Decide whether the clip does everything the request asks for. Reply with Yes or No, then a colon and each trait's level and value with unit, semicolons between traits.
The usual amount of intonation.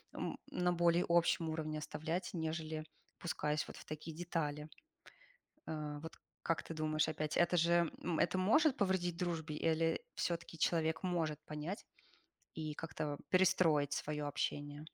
No: narrow, 2.1 semitones